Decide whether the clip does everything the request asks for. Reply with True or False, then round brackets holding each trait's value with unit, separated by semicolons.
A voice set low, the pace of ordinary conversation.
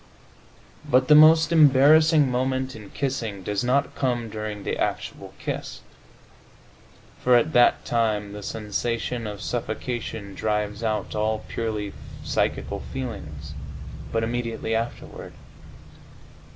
False (115 Hz; 110 wpm)